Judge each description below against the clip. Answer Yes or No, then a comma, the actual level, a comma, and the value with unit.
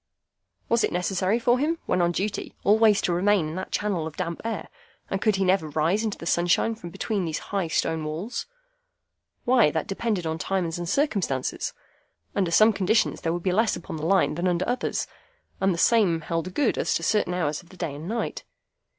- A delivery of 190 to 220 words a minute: Yes, fast, 205 wpm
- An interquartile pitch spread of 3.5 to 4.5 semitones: Yes, average, 4.2 semitones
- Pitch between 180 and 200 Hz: Yes, medium, 185 Hz